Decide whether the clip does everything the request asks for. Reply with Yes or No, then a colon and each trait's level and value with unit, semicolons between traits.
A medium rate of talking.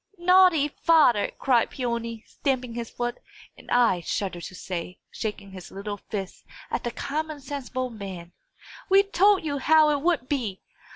Yes: average, 155 wpm